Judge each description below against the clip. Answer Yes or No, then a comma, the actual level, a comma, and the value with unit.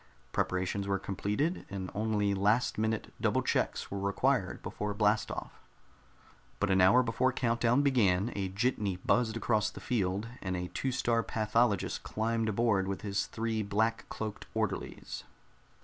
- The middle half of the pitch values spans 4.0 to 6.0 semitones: No, average, 2.8 semitones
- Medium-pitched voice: No, low, 105 Hz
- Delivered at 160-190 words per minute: No, average, 150 wpm